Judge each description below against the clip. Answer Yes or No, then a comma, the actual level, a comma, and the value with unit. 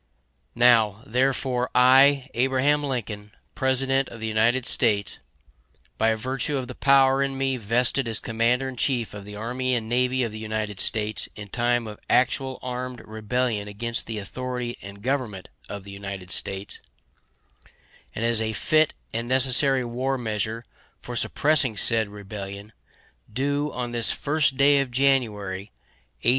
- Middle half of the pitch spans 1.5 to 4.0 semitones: Yes, average, 3.4 semitones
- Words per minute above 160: No, average, 150 wpm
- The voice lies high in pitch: No, low, 120 Hz